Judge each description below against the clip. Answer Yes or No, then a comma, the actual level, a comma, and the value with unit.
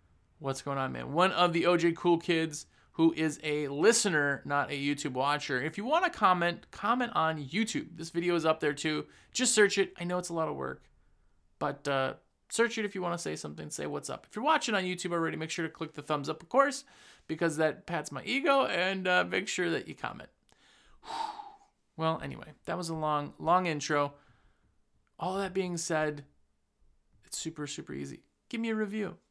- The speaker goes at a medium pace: No, fast, 210 wpm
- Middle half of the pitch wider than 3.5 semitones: Yes, average, 4.7 semitones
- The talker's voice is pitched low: No, medium, 165 Hz